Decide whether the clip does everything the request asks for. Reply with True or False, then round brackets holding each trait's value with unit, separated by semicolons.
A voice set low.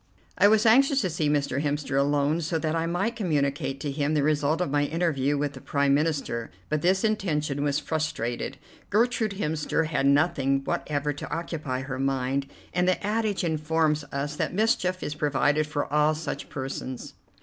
False (150 Hz)